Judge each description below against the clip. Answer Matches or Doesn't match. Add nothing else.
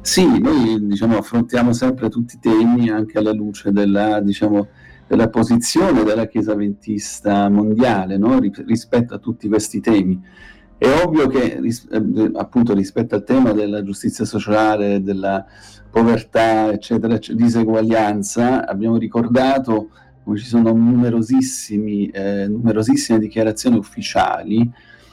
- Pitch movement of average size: Doesn't match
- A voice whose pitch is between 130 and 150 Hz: Doesn't match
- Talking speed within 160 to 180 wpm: Doesn't match